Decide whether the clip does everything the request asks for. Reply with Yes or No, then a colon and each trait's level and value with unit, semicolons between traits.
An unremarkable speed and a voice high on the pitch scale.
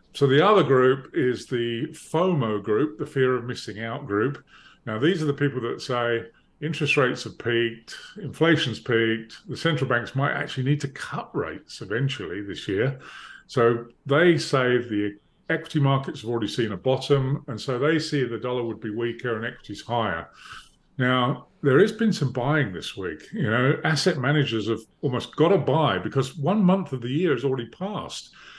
No: average, 185 wpm; low, 130 Hz